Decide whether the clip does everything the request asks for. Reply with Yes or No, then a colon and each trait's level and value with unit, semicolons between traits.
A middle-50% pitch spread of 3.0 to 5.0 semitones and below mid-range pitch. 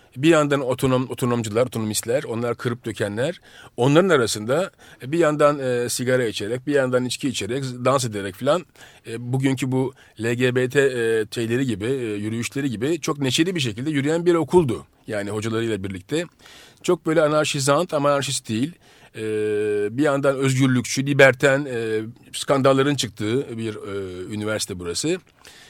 Yes: average, 3.8 semitones; low, 130 Hz